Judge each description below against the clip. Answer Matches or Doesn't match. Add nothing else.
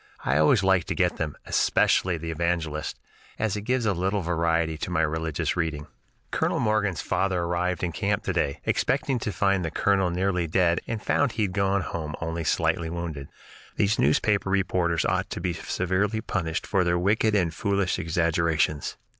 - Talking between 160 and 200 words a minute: Matches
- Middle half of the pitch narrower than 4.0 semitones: Matches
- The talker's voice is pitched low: Matches